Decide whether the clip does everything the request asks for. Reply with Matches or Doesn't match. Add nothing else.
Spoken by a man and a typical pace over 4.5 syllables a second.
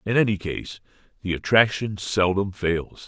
Doesn't match